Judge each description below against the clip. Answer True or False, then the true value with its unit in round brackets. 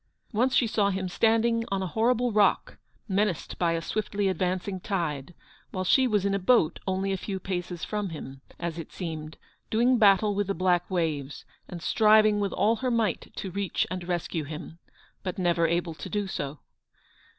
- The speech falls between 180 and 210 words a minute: True (185 wpm)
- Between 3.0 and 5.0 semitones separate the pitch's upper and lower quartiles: True (3.6 semitones)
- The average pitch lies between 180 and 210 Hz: True (190 Hz)